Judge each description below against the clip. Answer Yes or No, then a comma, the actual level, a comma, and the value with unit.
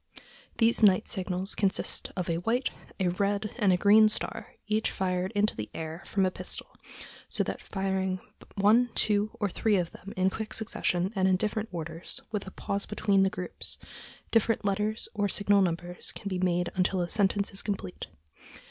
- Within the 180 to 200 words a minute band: Yes, average, 185 wpm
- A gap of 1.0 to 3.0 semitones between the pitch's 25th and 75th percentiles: Yes, narrow, 2.4 semitones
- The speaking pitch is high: Yes, high, 195 Hz